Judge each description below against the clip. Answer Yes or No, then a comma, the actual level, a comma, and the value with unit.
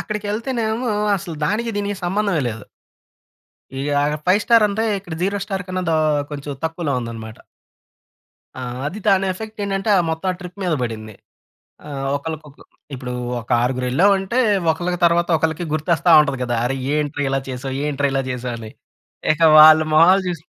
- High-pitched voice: No, medium, 165 Hz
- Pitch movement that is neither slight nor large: No, wide, 6.0 semitones